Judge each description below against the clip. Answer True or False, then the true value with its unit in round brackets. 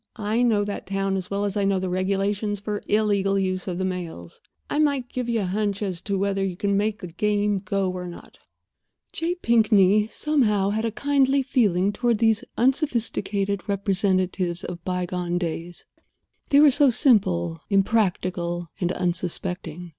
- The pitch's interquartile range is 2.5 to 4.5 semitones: True (3.1 semitones)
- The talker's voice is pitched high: True (200 Hz)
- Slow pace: False (170 wpm)